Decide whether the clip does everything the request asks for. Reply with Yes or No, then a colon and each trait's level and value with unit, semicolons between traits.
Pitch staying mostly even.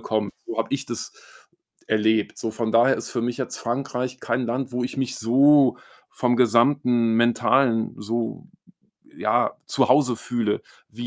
Yes: narrow, 2.1 semitones